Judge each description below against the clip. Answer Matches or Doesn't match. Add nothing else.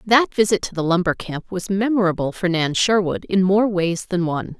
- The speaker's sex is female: Matches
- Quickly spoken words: Matches